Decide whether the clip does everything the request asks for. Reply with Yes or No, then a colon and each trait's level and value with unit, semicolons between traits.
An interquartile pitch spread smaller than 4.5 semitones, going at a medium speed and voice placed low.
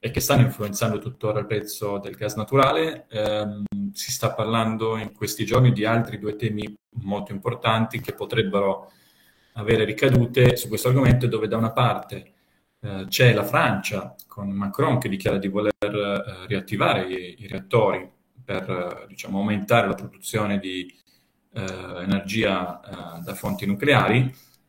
Yes: average, 3.2 semitones; average, 150 wpm; low, 105 Hz